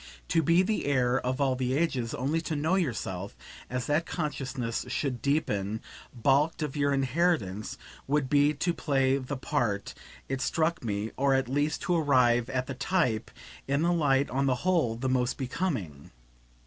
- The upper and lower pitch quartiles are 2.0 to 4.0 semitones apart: Yes, average, 3.4 semitones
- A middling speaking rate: Yes, average, 170 wpm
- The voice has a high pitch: No, low, 135 Hz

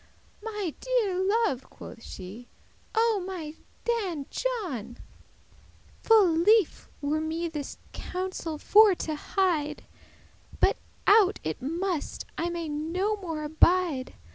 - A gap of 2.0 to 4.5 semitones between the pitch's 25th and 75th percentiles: No, average, 5.1 semitones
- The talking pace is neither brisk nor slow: No, slow, 115 wpm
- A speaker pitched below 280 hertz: No, very high, 345 Hz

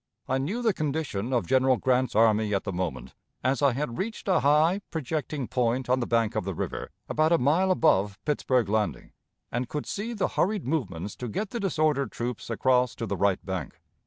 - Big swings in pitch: Yes, wide, 5.9 semitones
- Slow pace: No, average, 200 wpm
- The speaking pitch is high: No, low, 130 Hz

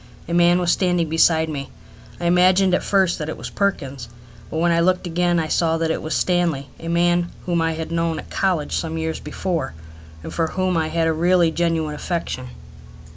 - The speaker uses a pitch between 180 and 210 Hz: No, medium, 170 Hz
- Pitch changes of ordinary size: No, narrow, 1.7 semitones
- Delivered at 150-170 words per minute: No, fast, 205 wpm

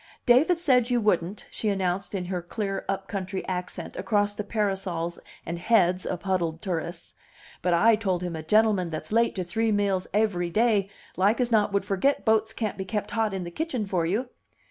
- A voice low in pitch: No, high, 195 Hz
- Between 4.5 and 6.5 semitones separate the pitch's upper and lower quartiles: No, average, 3.5 semitones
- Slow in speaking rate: No, average, 195 wpm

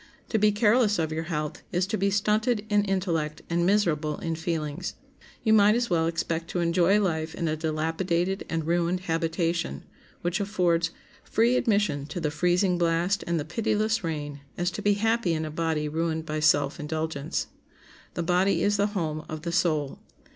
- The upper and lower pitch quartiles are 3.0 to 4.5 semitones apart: Yes, average, 4.1 semitones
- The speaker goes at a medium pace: Yes, average, 180 wpm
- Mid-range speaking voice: Yes, medium, 170 Hz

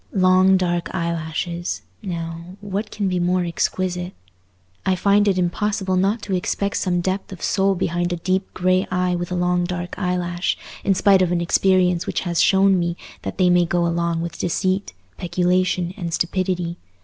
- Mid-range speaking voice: Yes, medium, 180 Hz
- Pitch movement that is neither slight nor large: No, narrow, 1.4 semitones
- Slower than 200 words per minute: Yes, average, 170 wpm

